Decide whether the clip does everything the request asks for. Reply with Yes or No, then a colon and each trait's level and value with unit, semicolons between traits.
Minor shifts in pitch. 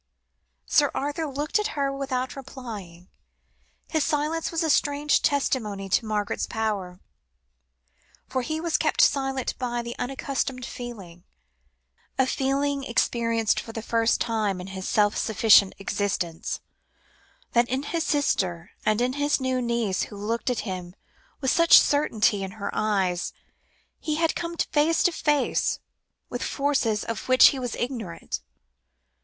No: wide, 5.4 semitones